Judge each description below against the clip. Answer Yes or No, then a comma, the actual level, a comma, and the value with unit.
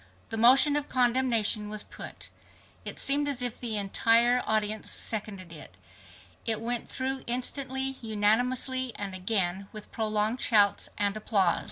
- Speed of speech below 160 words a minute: Yes, average, 140 wpm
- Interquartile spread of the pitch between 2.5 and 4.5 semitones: Yes, average, 3.5 semitones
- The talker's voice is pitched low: No, high, 225 Hz